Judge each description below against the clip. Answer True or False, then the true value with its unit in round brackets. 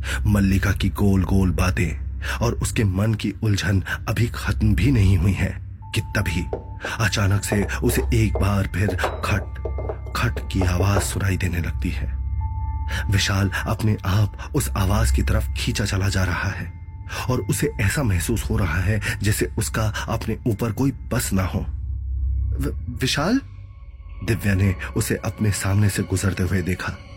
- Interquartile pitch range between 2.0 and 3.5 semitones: True (3.1 semitones)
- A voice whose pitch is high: False (95 Hz)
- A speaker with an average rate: True (155 wpm)